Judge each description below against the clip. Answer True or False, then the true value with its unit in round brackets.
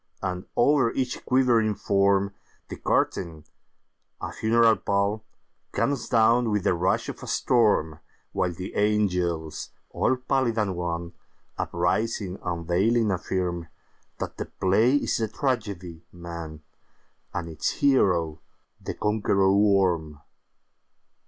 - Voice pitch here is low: True (100 Hz)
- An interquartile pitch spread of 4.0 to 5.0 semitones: True (4.4 semitones)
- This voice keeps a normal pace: False (100 wpm)